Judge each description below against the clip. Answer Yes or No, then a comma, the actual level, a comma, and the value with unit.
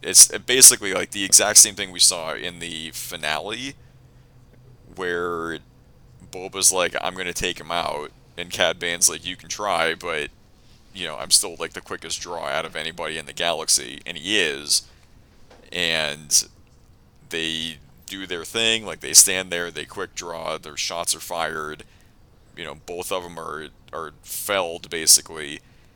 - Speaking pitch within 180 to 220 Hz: No, very low, 90 Hz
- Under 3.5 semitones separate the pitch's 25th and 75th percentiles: No, wide, 5.5 semitones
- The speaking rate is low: No, average, 160 wpm